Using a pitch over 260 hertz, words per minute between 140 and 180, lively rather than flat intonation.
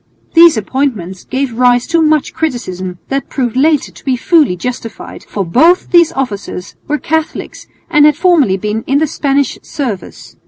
Yes: very high, 270 Hz; average, 160 wpm; wide, 6.1 semitones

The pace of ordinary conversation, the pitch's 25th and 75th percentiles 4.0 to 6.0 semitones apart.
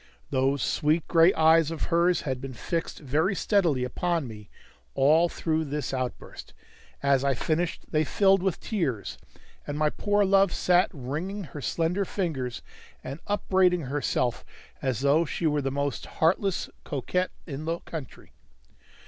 Yes: average, 150 wpm; average, 4.3 semitones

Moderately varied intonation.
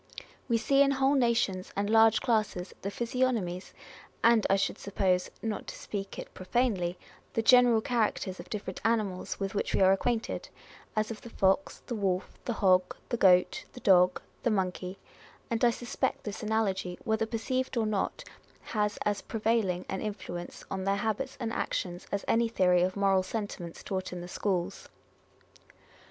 Yes: average, 3.4 semitones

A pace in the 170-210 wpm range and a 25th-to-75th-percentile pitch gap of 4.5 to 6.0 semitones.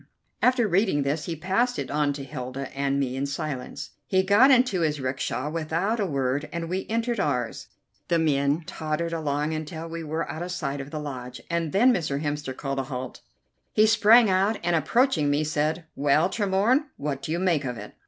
Yes: average, 200 wpm; average, 5.2 semitones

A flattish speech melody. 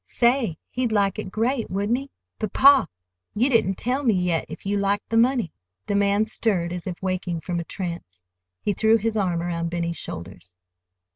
No: average, 4.5 semitones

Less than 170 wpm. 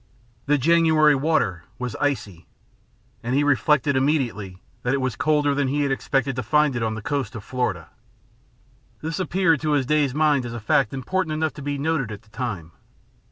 No: average, 190 wpm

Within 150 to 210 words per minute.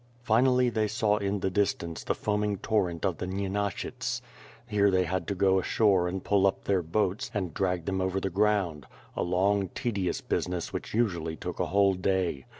Yes: average, 185 wpm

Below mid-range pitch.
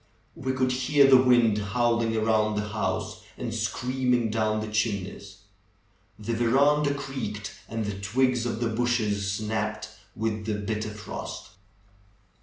Yes: low, 110 Hz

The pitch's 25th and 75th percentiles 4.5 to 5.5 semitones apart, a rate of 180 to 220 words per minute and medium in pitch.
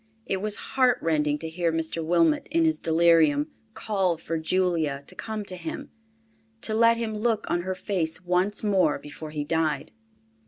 No: average, 5.2 semitones; average, 160 wpm; medium, 180 Hz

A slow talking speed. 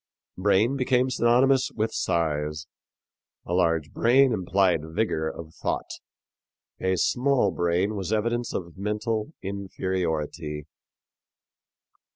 Yes: slow, 100 wpm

